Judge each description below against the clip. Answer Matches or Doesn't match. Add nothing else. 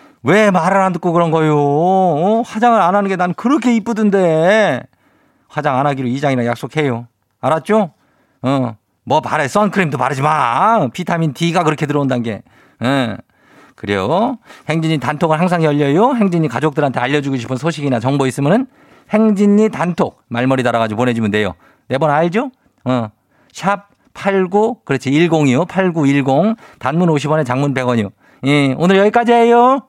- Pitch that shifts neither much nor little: Doesn't match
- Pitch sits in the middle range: Matches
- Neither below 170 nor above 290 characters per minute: Doesn't match